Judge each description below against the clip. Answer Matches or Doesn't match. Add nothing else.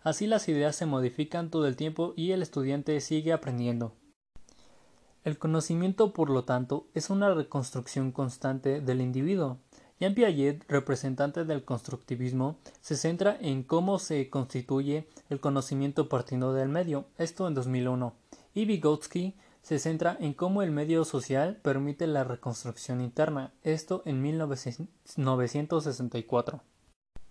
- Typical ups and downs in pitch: Matches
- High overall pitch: Doesn't match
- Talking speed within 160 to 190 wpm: Doesn't match